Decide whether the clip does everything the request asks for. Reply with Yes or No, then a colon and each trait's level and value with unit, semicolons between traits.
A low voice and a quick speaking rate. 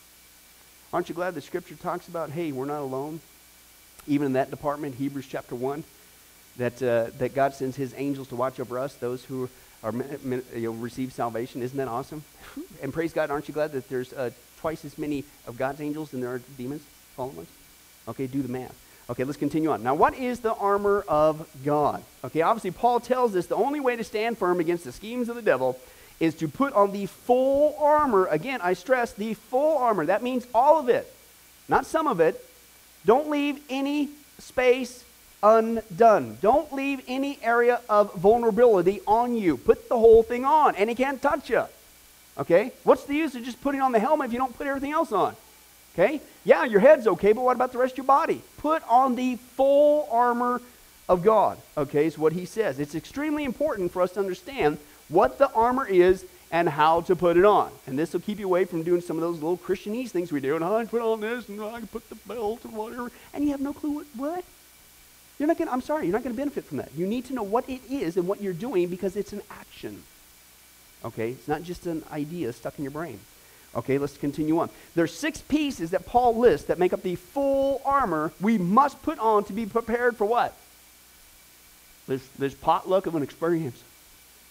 No: medium, 185 Hz; fast, 215 wpm